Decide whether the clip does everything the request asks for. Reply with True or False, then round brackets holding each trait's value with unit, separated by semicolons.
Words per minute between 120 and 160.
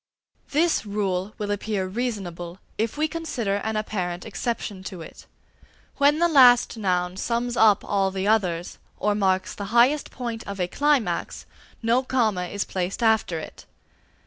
True (150 wpm)